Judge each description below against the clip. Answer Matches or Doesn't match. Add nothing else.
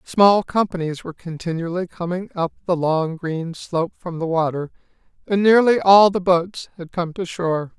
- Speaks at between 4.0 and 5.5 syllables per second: Matches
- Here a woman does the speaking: Doesn't match